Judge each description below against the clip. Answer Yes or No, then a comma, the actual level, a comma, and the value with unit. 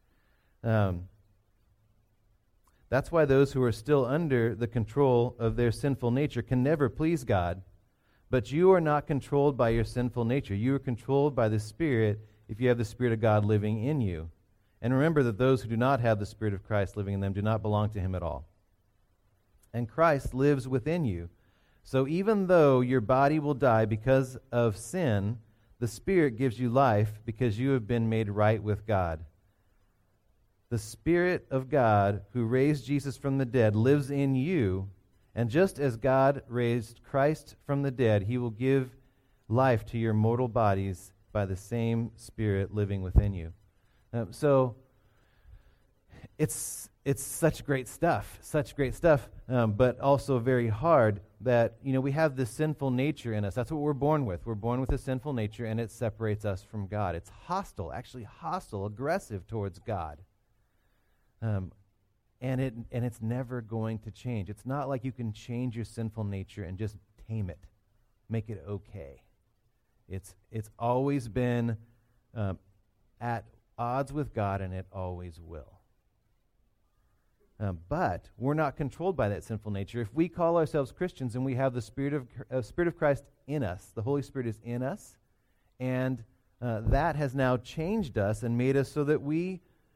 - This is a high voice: No, low, 115 Hz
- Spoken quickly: No, average, 175 wpm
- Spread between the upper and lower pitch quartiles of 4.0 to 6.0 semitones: Yes, average, 4.3 semitones